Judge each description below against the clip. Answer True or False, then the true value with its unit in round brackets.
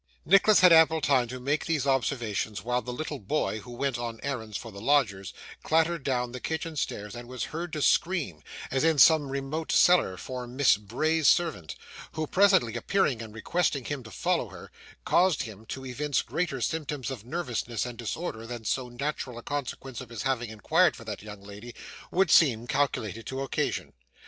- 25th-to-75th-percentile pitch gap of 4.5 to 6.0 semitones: True (5.2 semitones)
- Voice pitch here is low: True (130 Hz)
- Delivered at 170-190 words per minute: True (185 wpm)